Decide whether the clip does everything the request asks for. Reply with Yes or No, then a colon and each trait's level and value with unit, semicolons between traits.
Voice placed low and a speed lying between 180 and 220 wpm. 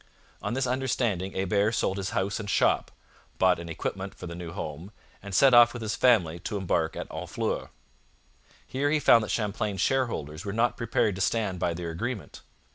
Yes: low, 100 Hz; average, 190 wpm